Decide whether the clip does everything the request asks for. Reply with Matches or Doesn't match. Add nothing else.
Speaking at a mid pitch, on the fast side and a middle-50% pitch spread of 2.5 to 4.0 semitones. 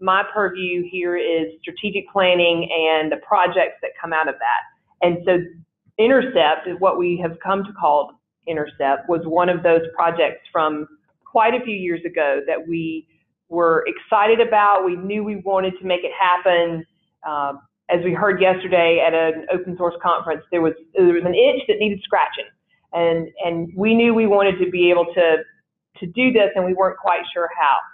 Doesn't match